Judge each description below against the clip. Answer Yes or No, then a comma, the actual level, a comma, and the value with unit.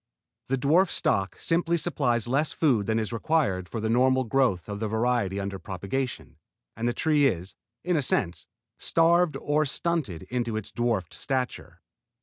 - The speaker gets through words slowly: No, average, 160 wpm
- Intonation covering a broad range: Yes, wide, 6.0 semitones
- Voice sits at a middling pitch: No, low, 125 Hz